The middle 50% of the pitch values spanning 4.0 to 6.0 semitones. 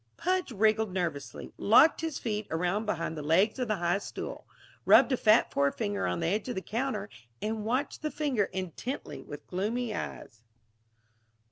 Yes: average, 5.2 semitones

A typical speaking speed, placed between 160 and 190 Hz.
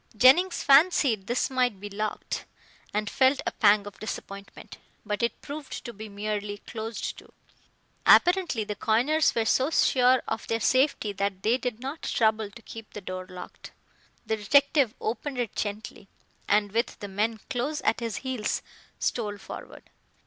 No: average, 160 wpm; high, 225 Hz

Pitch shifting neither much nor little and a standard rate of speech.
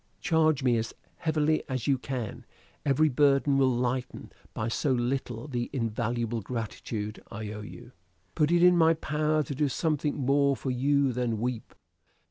Yes: average, 3.8 semitones; average, 160 wpm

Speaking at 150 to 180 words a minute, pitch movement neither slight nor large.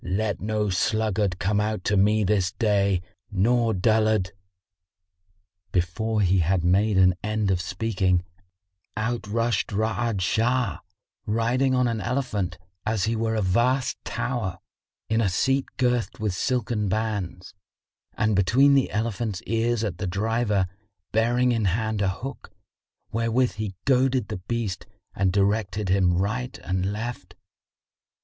No: slow, 135 wpm; average, 3.3 semitones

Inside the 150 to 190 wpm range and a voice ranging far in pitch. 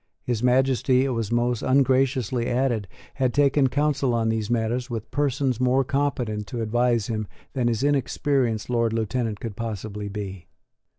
No: average, 155 wpm; average, 2.9 semitones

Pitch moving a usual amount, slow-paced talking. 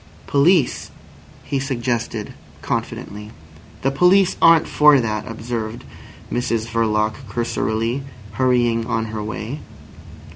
Yes: average, 3.5 semitones; slow, 100 wpm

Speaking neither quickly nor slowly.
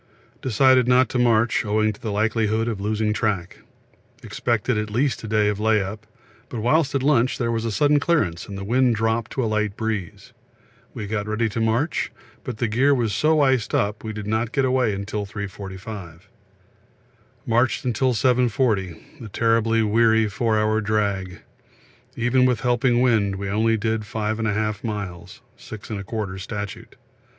Yes: average, 160 wpm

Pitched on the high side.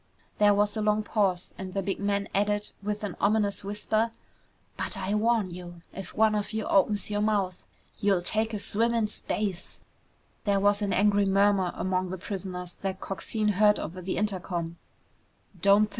Yes: high, 200 Hz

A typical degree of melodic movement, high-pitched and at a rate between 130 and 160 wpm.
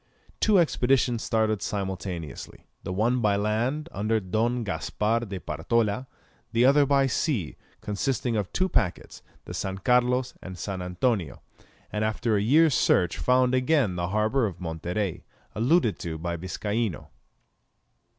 No: average, 4.9 semitones; low, 110 Hz; average, 140 wpm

